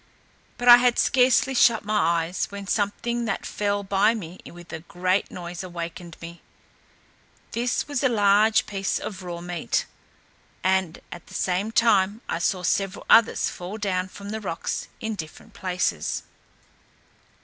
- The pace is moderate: Yes, average, 150 wpm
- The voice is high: Yes, high, 195 Hz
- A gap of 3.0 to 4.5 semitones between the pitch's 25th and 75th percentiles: Yes, average, 3.7 semitones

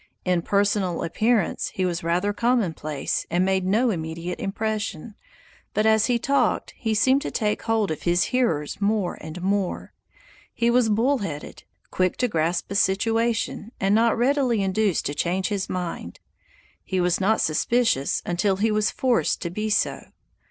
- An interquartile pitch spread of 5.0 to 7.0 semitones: No, average, 4.1 semitones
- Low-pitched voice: No, high, 200 Hz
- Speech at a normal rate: Yes, average, 160 wpm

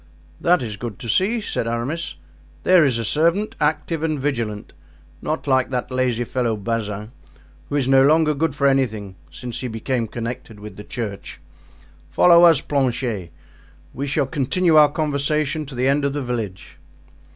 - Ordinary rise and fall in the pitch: Yes, average, 4.6 semitones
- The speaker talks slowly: No, average, 165 wpm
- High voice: No, low, 135 Hz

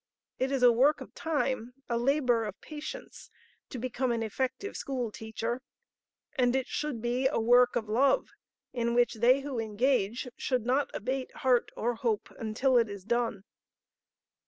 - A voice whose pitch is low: No, high, 245 Hz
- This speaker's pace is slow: No, average, 160 wpm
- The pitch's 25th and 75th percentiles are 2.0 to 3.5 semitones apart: Yes, narrow, 2.5 semitones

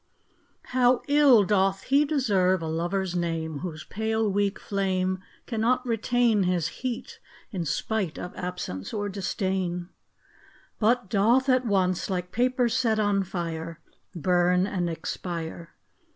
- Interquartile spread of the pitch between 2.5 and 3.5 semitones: No, average, 4.2 semitones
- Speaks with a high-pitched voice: Yes, high, 195 Hz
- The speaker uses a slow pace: Yes, slow, 125 wpm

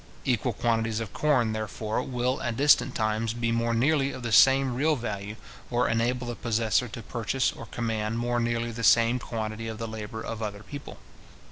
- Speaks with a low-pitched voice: Yes, low, 115 Hz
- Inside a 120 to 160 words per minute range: No, average, 190 wpm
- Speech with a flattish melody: Yes, narrow, 1.9 semitones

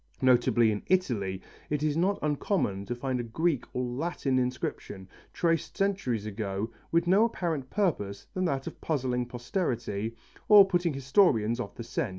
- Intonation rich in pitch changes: Yes, wide, 6.7 semitones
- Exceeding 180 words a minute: No, average, 160 wpm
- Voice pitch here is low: Yes, low, 130 Hz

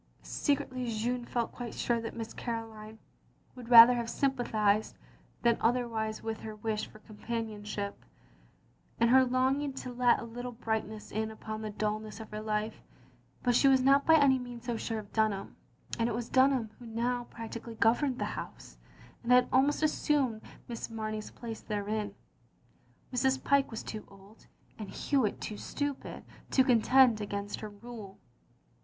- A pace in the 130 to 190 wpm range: Yes, average, 165 wpm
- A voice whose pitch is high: Yes, high, 230 Hz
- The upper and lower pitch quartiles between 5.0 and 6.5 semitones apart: No, narrow, 2.5 semitones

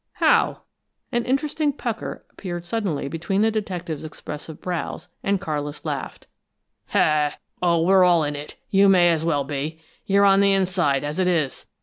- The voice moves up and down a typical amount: Yes, average, 4.4 semitones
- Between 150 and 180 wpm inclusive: Yes, average, 155 wpm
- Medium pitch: Yes, medium, 175 Hz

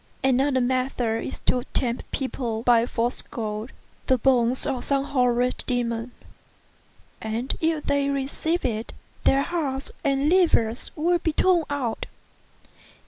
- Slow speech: Yes, slow, 130 wpm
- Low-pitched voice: No, very high, 260 Hz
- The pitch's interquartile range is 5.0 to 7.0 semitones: No, average, 3.0 semitones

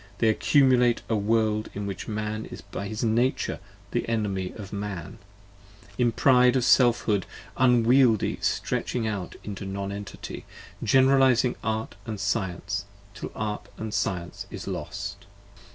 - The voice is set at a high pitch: No, low, 110 Hz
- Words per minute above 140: No, slow, 135 wpm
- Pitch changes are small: No, average, 3.3 semitones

